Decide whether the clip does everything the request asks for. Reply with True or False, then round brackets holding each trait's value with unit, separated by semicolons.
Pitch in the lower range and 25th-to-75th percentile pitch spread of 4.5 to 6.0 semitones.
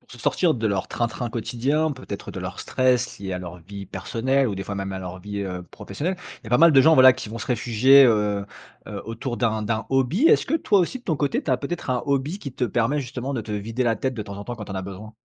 True (120 Hz; 4.8 semitones)